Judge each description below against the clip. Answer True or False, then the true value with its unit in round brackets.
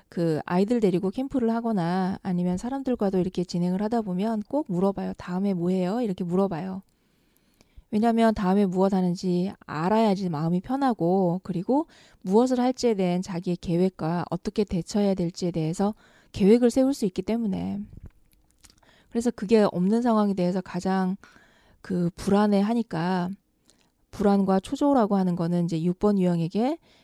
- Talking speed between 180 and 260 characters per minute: False (340 characters per minute)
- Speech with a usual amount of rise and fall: True (3.8 semitones)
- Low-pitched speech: False (190 Hz)